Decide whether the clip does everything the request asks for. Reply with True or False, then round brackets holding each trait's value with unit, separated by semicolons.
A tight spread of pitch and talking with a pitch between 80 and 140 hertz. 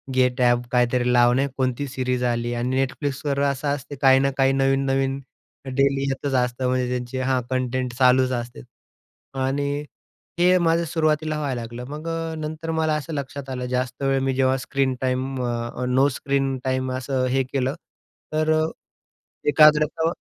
True (2.1 semitones; 135 Hz)